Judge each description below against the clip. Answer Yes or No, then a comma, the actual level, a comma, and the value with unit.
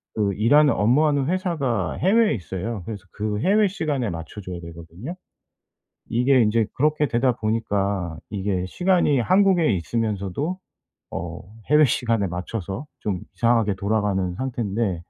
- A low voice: Yes, low, 115 Hz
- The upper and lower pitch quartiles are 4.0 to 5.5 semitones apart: No, wide, 6.8 semitones